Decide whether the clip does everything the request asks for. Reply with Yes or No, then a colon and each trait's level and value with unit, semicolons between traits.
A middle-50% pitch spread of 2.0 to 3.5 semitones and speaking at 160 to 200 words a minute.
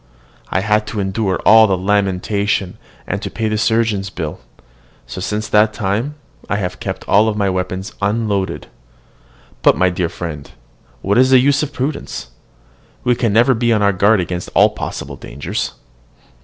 Yes: average, 3.1 semitones; average, 165 wpm